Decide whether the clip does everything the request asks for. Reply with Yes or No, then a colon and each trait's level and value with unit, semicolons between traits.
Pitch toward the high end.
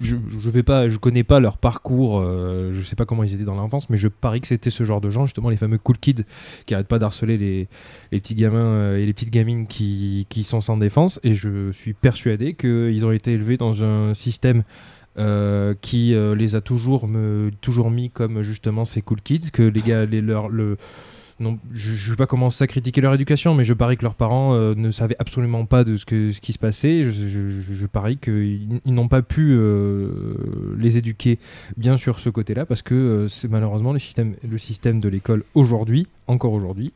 No: low, 115 Hz